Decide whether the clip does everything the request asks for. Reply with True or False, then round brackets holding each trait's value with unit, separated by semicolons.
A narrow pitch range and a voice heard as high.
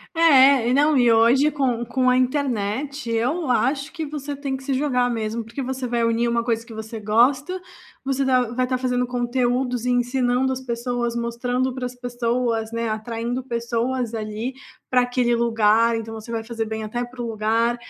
True (2.1 semitones; 245 Hz)